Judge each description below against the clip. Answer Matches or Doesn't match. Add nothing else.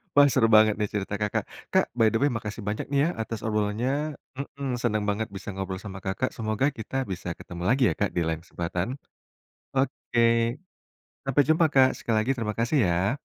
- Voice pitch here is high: Doesn't match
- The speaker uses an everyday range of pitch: Matches